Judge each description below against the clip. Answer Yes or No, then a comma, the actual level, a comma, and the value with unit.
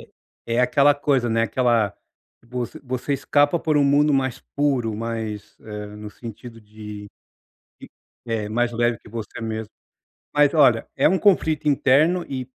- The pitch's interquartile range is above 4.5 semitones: No, average, 4.2 semitones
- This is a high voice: No, low, 120 Hz